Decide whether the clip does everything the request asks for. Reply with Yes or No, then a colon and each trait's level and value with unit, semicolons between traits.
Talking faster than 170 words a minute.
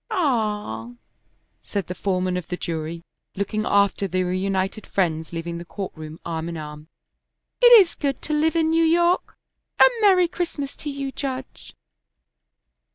No: average, 155 wpm